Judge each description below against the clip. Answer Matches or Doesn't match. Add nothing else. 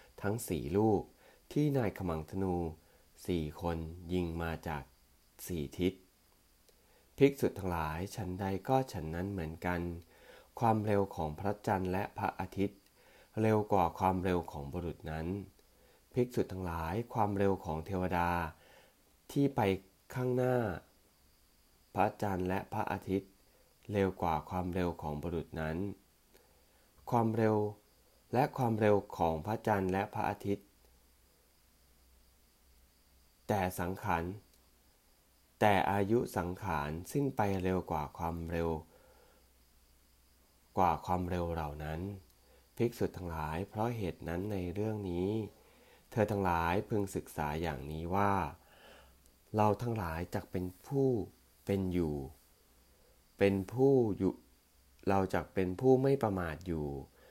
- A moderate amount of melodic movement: Matches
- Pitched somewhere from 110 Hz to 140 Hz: Doesn't match